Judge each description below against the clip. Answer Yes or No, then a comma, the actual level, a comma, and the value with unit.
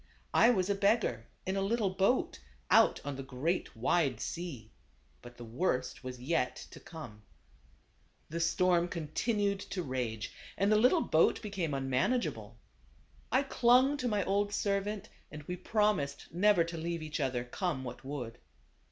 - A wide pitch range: Yes, wide, 7.5 semitones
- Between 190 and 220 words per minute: No, average, 155 wpm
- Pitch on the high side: No, medium, 170 Hz